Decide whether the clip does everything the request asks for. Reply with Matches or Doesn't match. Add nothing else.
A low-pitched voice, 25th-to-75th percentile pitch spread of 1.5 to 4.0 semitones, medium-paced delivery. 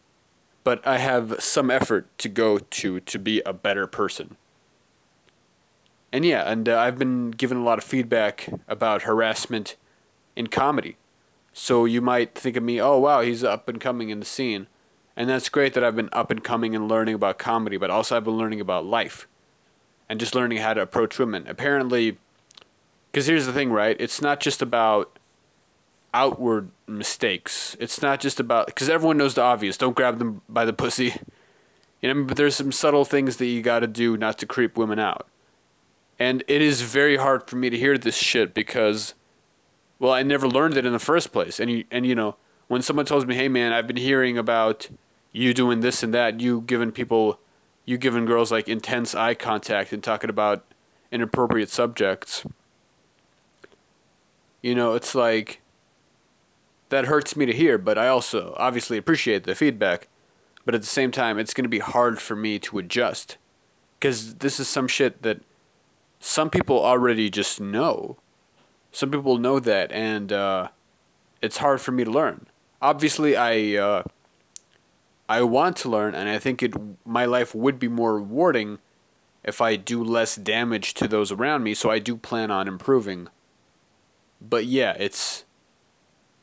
Matches